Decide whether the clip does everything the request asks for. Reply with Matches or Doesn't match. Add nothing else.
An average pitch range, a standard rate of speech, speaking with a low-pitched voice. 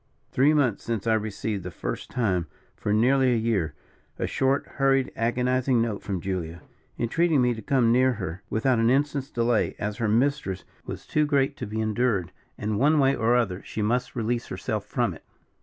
Matches